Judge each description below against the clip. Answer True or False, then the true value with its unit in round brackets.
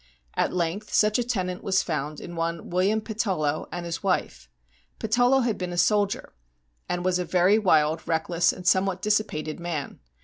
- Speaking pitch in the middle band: True (180 Hz)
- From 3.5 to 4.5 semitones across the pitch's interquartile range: True (3.8 semitones)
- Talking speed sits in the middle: True (175 wpm)